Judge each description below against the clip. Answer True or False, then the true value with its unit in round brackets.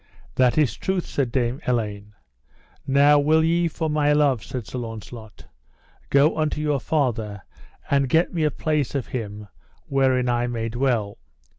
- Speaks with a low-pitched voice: True (130 Hz)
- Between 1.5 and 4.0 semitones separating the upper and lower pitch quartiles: False (4.4 semitones)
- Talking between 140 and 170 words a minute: True (155 wpm)